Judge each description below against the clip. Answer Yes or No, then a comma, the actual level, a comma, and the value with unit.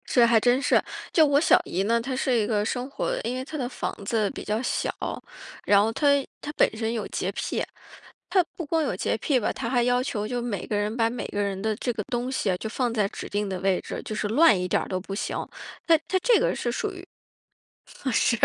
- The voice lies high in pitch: Yes, high, 235 Hz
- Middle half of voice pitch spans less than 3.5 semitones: No, average, 3.8 semitones